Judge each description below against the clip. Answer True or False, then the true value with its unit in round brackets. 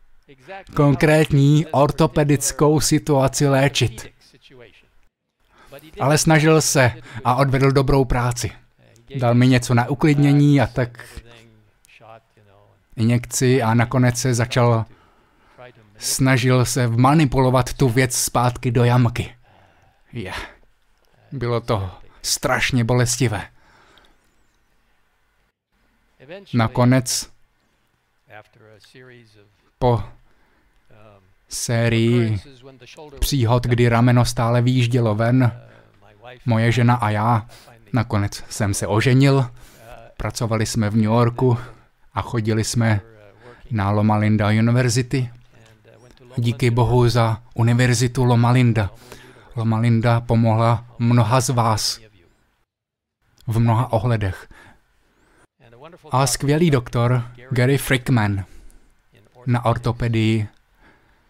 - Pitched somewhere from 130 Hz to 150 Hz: False (120 Hz)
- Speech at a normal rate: False (85 wpm)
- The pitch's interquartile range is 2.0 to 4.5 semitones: True (2.4 semitones)